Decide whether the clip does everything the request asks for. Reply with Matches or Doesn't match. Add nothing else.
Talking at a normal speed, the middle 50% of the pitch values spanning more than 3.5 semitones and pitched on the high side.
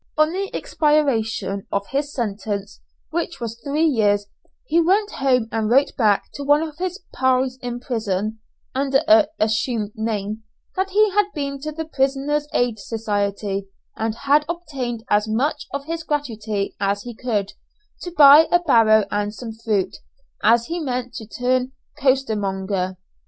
Matches